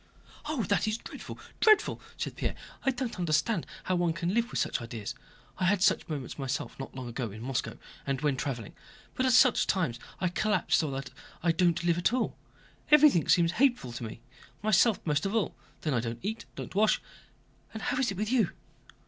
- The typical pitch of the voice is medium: Yes, medium, 175 Hz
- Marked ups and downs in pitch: Yes, wide, 8.3 semitones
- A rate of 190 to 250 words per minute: Yes, average, 200 wpm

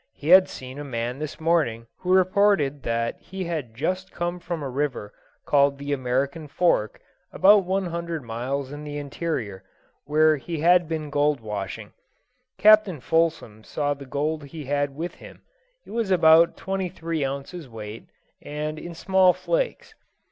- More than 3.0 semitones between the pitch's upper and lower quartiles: Yes, average, 4.3 semitones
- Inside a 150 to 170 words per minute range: Yes, average, 160 wpm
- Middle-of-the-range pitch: Yes, medium, 150 Hz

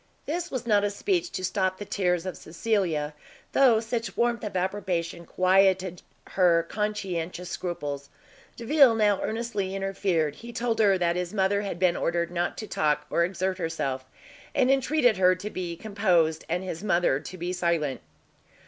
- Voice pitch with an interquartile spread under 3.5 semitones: No, average, 3.8 semitones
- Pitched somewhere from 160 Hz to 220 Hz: Yes, medium, 185 Hz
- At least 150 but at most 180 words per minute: Yes, average, 165 wpm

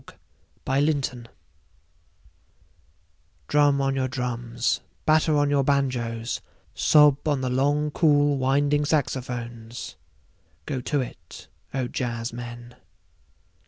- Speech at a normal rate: No, slow, 95 wpm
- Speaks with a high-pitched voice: No, low, 135 Hz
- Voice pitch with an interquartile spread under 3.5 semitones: Yes, average, 3.1 semitones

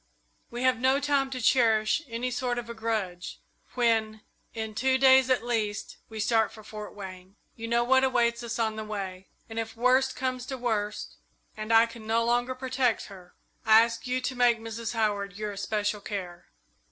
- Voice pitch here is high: Yes, high, 230 Hz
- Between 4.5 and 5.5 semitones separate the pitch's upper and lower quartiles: No, average, 2.7 semitones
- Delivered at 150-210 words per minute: Yes, average, 190 wpm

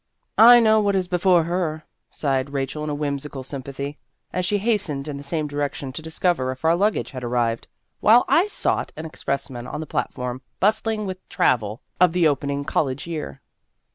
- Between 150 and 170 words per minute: No, average, 180 wpm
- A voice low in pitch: No, medium, 150 Hz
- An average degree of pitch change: Yes, average, 5.0 semitones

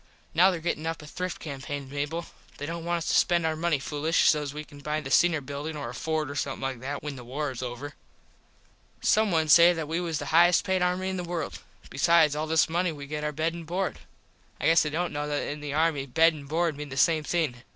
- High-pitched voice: No, medium, 155 Hz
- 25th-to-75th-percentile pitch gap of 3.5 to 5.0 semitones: No, average, 2.7 semitones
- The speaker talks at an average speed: No, fast, 255 wpm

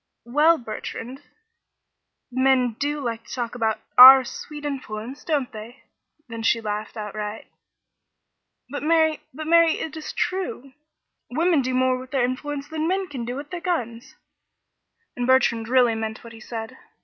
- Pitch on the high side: Yes, very high, 255 Hz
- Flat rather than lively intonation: No, average, 4.3 semitones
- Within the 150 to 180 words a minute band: Yes, average, 155 wpm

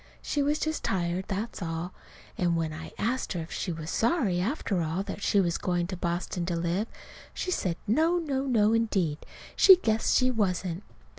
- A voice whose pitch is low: No, high, 190 Hz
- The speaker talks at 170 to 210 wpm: Yes, average, 190 wpm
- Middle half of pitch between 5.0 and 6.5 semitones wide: Yes, average, 5.3 semitones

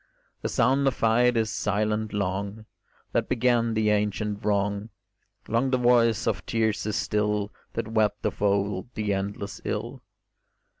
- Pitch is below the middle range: Yes, low, 105 Hz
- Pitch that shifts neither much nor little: No, narrow, 2.0 semitones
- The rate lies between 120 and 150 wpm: Yes, average, 145 wpm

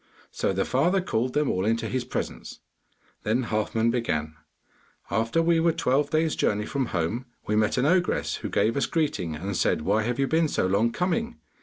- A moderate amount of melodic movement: No, wide, 6.7 semitones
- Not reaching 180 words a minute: No, average, 190 wpm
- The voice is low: Yes, low, 120 Hz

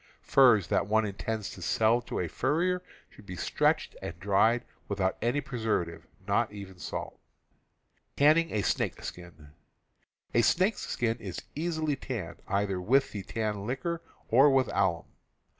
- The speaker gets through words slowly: Yes, slow, 130 wpm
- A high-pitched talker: No, low, 110 Hz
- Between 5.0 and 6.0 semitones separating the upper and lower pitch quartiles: Yes, wide, 5.6 semitones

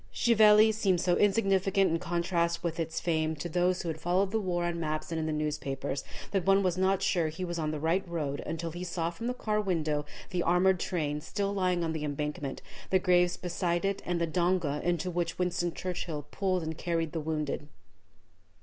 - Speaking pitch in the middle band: Yes, medium, 175 Hz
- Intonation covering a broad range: No, average, 2.7 semitones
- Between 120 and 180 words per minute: No, fast, 205 wpm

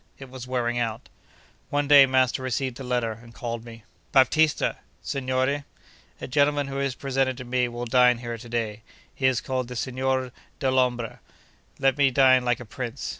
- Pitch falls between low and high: No, low, 130 Hz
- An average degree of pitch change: No, narrow, 1.9 semitones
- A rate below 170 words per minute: No, average, 175 wpm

